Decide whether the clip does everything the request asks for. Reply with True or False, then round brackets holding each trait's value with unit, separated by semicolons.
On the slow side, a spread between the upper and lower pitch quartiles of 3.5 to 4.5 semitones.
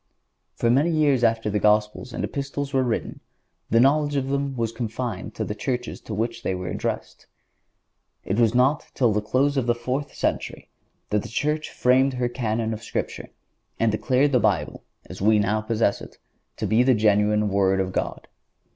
False (185 wpm; 3.8 semitones)